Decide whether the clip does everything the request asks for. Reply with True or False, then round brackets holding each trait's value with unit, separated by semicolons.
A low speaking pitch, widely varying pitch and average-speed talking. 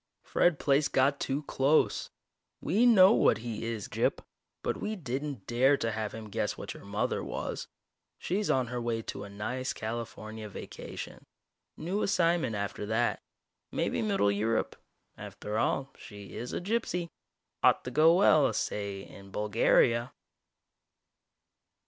True (120 Hz; 6.1 semitones; 145 wpm)